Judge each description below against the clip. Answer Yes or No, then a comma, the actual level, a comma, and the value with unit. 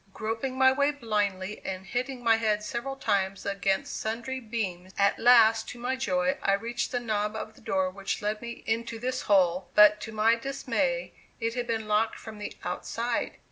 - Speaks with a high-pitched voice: Yes, high, 225 Hz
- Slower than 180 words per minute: No, average, 185 wpm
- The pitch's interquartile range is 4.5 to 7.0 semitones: No, average, 2.9 semitones